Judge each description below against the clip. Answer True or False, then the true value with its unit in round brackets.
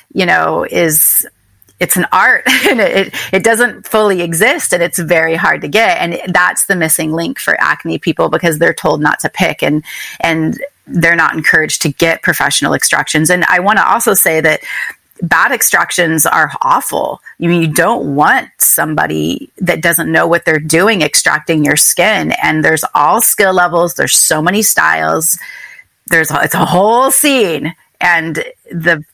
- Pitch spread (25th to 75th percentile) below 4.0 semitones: True (3.0 semitones)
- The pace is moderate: True (175 wpm)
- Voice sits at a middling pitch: True (170 Hz)